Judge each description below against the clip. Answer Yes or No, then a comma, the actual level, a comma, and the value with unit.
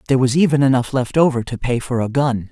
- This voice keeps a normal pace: No, fast, 260 wpm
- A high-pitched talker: No, low, 130 Hz